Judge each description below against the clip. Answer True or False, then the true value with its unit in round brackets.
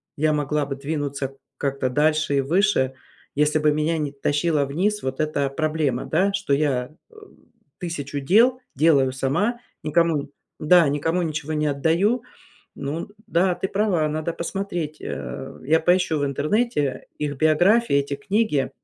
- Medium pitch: True (155 Hz)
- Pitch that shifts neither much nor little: True (3.7 semitones)